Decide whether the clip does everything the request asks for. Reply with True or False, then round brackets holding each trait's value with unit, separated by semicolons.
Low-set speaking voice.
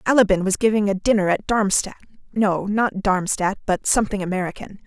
False (200 Hz)